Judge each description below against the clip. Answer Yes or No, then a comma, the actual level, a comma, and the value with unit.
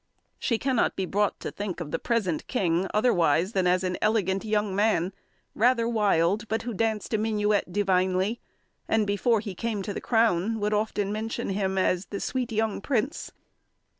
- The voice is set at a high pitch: Yes, high, 210 Hz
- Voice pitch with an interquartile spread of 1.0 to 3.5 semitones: Yes, average, 2.8 semitones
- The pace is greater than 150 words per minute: Yes, average, 175 wpm